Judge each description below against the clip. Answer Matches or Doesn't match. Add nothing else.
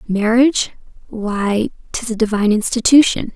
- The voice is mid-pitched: Doesn't match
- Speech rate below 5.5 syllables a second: Matches